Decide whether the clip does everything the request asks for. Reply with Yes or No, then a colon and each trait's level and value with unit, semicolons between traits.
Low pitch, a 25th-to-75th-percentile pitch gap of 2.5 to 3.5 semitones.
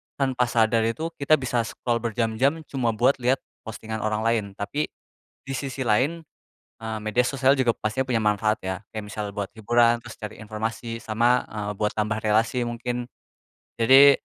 Yes: low, 115 Hz; average, 2.8 semitones